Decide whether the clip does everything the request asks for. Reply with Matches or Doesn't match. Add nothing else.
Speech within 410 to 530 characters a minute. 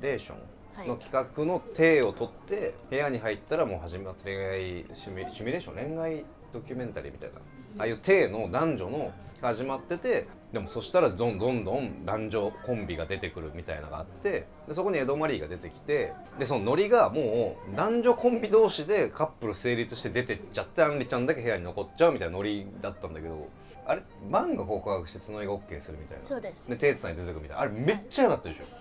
Matches